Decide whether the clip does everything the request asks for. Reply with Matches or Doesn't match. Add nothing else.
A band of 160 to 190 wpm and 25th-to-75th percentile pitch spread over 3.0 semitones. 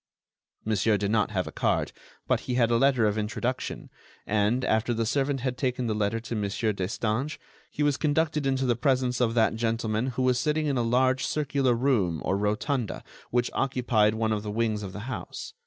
Doesn't match